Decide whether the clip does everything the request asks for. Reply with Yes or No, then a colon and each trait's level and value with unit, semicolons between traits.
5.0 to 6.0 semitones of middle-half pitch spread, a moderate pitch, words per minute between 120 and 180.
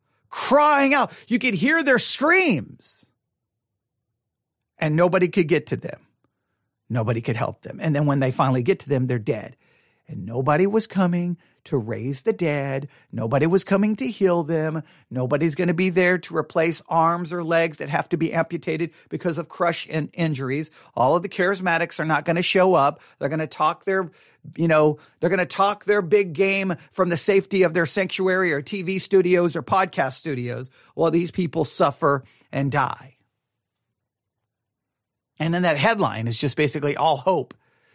Yes: wide, 5.4 semitones; medium, 165 Hz; average, 175 wpm